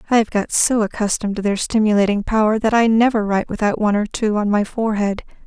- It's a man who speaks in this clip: No, female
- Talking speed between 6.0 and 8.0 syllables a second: Yes, 6.5 syllables/s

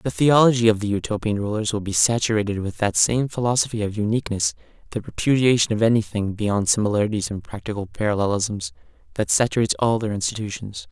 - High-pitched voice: No, low, 110 Hz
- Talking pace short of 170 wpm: Yes, average, 160 wpm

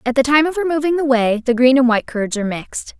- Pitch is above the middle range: Yes, very high, 260 Hz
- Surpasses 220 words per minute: Yes, fast, 280 wpm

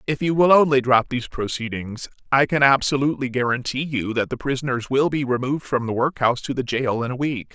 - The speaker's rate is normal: No, fast, 215 wpm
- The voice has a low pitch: Yes, low, 130 Hz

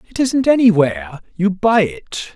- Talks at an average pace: Yes, average, 155 wpm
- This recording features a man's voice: Yes, male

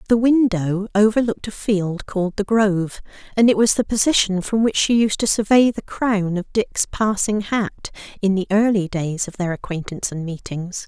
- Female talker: Yes, female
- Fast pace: No, average, 190 wpm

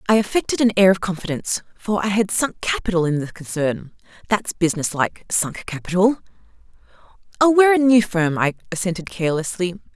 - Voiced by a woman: Yes, female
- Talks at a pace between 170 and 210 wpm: No, average, 150 wpm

